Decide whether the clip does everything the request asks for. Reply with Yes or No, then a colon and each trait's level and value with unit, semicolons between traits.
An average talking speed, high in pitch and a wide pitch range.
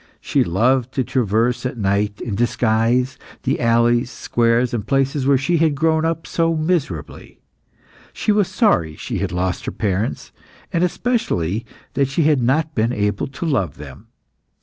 No: average, 160 wpm; low, 125 Hz; wide, 6.2 semitones